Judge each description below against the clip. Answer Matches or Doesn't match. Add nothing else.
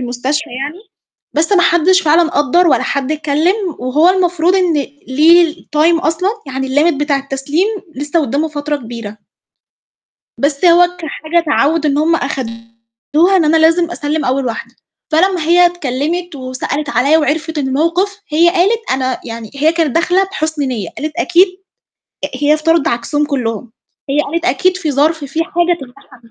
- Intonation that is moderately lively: Matches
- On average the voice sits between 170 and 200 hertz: Doesn't match